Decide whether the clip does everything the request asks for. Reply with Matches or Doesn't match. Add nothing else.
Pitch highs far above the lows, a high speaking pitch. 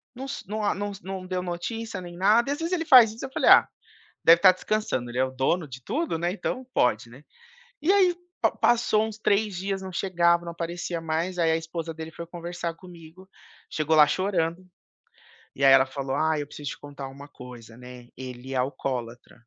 Doesn't match